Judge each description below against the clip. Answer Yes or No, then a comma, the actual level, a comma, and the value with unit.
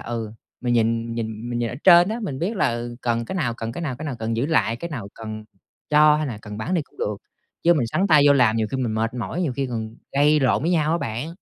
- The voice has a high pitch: No, low, 125 Hz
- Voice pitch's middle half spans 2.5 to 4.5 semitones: No, average, 5.2 semitones